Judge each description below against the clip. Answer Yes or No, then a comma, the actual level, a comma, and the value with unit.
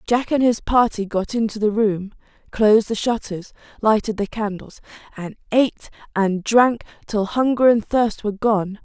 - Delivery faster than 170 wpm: No, average, 165 wpm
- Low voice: No, high, 215 Hz